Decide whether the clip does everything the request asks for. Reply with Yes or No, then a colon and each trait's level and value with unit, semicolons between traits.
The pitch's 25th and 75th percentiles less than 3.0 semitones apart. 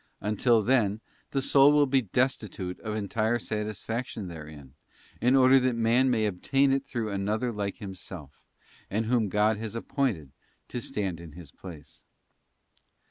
No: average, 4.6 semitones